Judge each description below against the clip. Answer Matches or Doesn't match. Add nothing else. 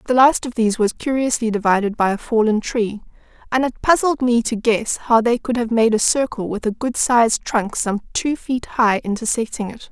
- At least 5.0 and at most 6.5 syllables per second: Matches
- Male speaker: Doesn't match